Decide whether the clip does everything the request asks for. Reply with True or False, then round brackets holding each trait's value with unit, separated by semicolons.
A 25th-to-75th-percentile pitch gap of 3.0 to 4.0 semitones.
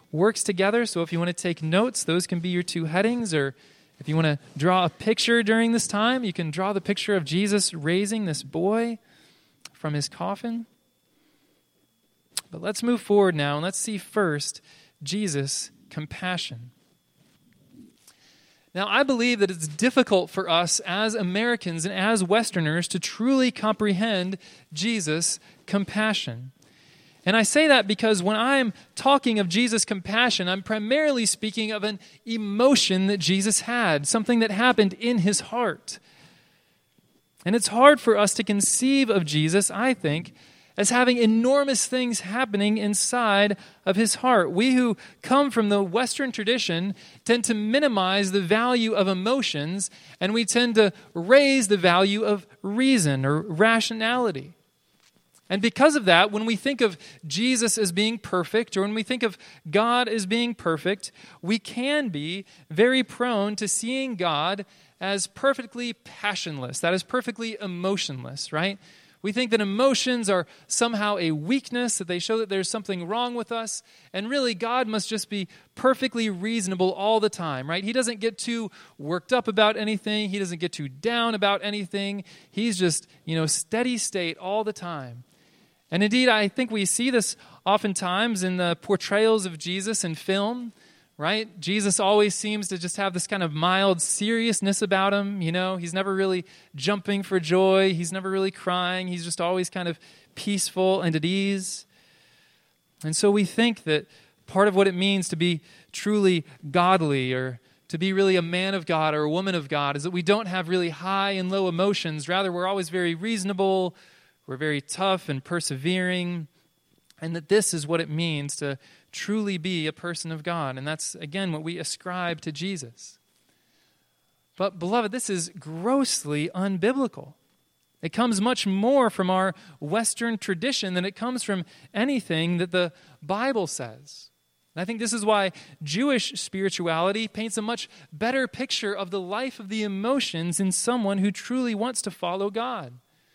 False (4.5 semitones)